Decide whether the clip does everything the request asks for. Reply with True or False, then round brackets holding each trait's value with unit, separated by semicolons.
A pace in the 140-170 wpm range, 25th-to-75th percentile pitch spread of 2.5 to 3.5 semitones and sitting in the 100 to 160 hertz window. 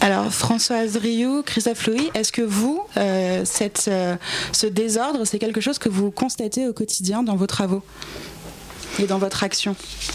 False (165 wpm; 2.9 semitones; 220 Hz)